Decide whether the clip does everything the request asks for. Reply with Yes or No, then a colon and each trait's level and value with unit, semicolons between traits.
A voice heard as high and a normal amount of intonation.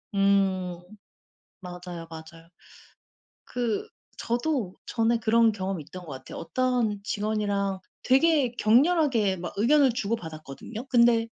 Yes: high, 215 Hz; average, 4.6 semitones